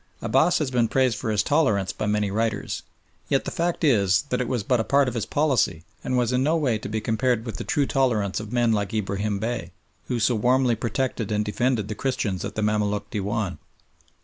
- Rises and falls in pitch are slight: No, average, 3.5 semitones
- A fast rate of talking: Yes, fast, 220 wpm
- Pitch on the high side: No, low, 115 Hz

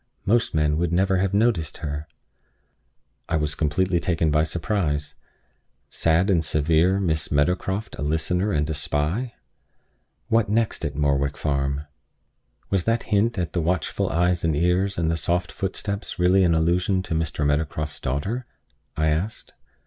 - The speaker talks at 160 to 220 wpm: No, average, 150 wpm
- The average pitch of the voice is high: No, very low, 85 Hz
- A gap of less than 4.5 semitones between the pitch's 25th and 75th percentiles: Yes, average, 4.0 semitones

